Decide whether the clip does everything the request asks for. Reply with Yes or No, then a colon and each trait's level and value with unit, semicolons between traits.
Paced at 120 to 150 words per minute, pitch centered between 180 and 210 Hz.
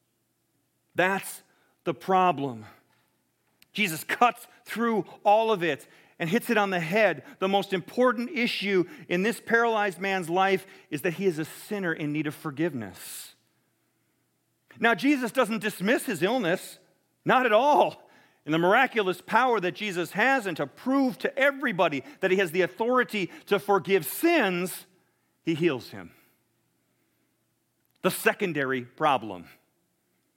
Yes: slow, 135 wpm; medium, 185 Hz